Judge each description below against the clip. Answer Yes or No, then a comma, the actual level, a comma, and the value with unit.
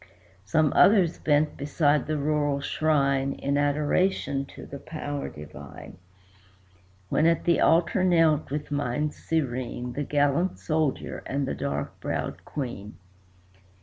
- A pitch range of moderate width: No, narrow, 2.2 semitones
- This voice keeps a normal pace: No, slow, 125 wpm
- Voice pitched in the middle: Yes, medium, 145 Hz